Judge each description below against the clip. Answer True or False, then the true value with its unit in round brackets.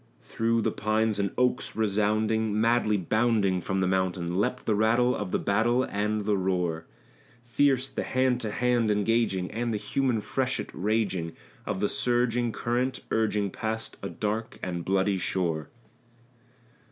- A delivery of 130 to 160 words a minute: True (150 wpm)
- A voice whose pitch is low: True (110 Hz)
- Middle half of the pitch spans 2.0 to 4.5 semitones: True (3.4 semitones)